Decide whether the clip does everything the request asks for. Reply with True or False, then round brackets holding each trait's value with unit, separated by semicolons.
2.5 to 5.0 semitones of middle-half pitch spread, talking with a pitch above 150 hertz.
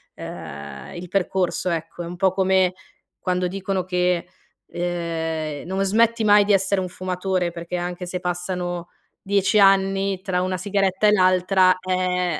False (1.6 semitones; 185 Hz)